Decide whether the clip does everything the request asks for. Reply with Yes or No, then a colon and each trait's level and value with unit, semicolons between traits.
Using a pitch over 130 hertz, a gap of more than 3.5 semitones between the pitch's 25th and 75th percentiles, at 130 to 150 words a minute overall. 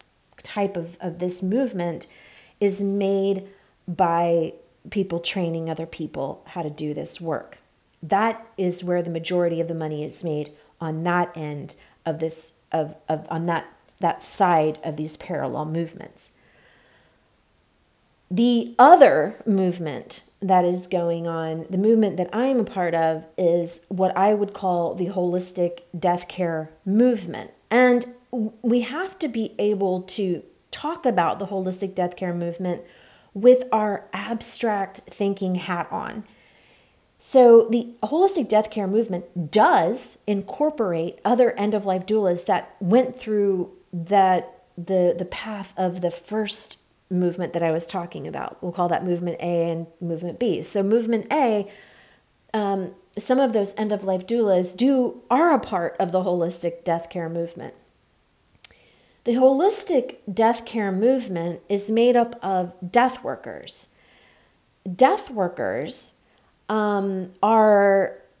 Yes: medium, 185 Hz; average, 4.1 semitones; slow, 135 wpm